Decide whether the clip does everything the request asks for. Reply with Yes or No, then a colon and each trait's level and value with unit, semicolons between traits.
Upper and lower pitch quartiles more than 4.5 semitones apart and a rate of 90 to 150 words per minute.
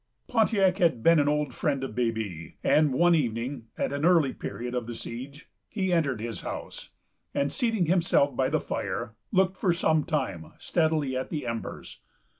No: wide, 5.6 semitones; average, 175 wpm